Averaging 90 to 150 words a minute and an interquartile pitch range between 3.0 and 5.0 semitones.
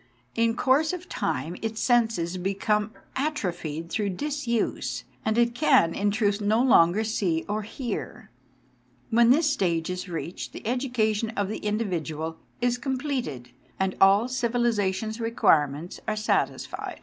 Yes: slow, 135 wpm; average, 4.7 semitones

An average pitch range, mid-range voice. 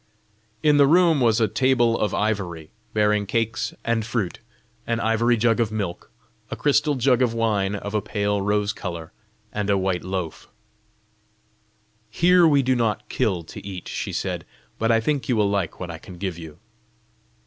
No: average, 3.5 semitones; low, 110 Hz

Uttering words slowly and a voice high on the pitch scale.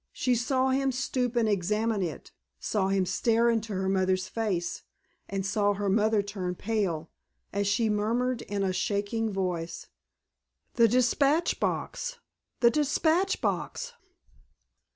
Yes: slow, 130 wpm; high, 215 Hz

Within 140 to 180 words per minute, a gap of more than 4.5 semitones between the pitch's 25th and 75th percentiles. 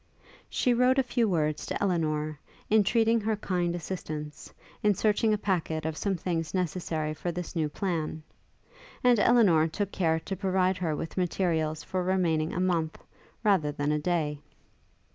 No: average, 160 wpm; average, 4.1 semitones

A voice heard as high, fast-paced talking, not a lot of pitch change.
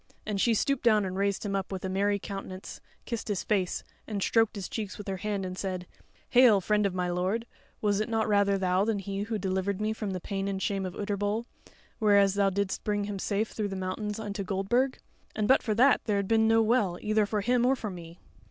Yes: high, 205 Hz; fast, 235 wpm; narrow, 2.0 semitones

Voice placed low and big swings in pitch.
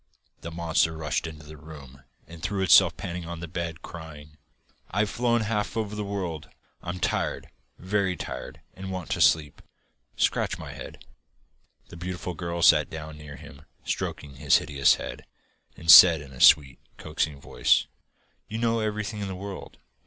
No: very low, 85 Hz; average, 3.9 semitones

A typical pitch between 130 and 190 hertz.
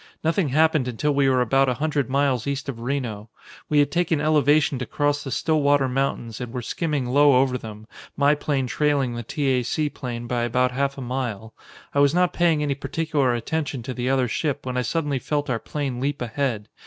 Yes: low, 135 Hz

